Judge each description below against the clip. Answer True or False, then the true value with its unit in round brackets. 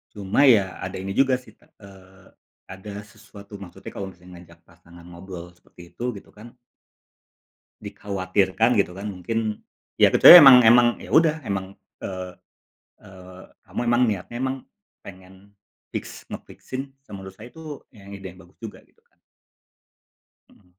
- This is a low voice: True (100 Hz)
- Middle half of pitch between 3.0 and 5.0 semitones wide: True (3.5 semitones)